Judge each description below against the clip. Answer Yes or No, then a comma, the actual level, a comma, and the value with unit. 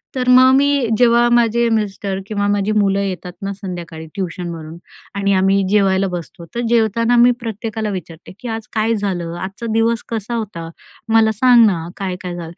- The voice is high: Yes, high, 205 Hz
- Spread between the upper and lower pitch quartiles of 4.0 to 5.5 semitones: No, average, 3.6 semitones